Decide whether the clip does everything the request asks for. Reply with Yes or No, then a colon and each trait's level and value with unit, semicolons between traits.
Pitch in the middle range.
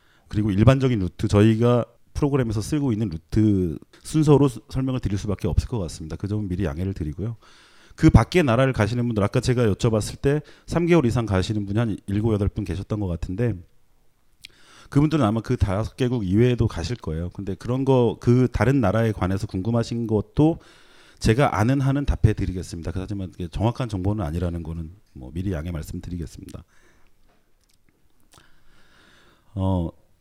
No: low, 105 Hz